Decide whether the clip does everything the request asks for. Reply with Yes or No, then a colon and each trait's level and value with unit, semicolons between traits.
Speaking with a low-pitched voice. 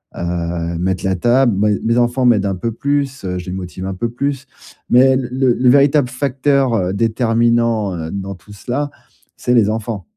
Yes: low, 115 Hz